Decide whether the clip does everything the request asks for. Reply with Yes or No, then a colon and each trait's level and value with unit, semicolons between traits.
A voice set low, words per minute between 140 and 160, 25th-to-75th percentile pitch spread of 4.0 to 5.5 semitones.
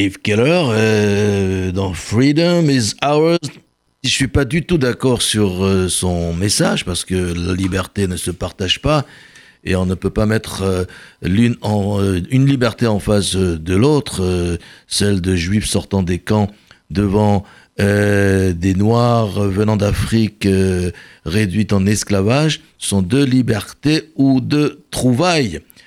Yes: low, 100 Hz; average, 150 wpm; average, 4.4 semitones